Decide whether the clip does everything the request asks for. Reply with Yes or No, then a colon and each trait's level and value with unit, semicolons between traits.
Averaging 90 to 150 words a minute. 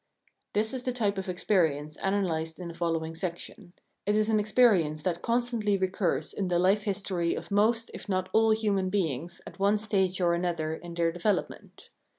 No: average, 180 wpm